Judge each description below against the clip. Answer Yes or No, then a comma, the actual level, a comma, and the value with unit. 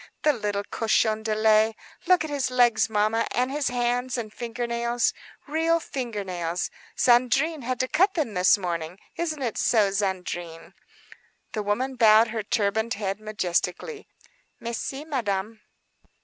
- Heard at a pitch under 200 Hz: No, high, 225 Hz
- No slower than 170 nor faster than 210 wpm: No, average, 145 wpm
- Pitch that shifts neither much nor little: Yes, average, 3.7 semitones